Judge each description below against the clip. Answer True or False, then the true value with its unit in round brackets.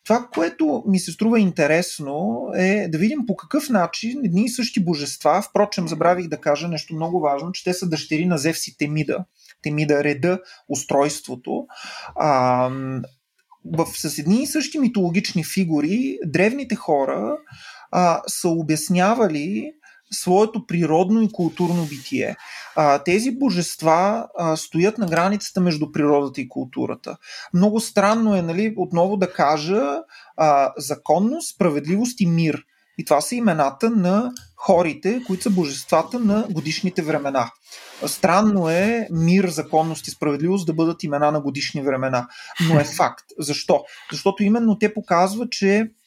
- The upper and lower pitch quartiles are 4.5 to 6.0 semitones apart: True (5.1 semitones)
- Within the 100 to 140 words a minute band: True (135 wpm)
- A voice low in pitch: False (175 Hz)